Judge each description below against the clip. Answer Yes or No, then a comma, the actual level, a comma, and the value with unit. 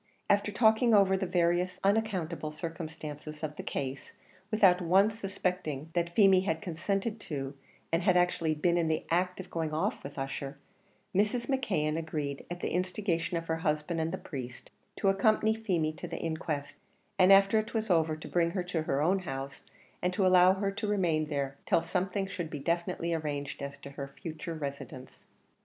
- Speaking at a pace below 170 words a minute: No, average, 185 wpm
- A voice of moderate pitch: Yes, medium, 170 Hz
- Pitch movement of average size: Yes, average, 4.0 semitones